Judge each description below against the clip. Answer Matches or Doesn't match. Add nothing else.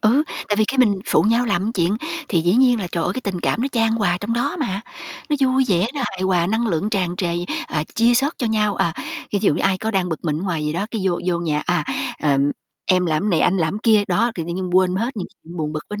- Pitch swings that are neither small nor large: Matches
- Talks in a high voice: Matches